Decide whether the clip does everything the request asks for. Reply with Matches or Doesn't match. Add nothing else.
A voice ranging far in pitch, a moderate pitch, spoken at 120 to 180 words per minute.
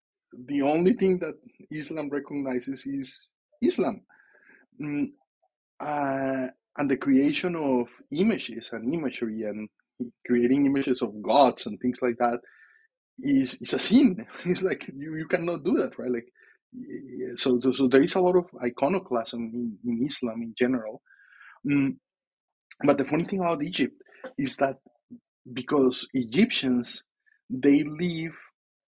Matches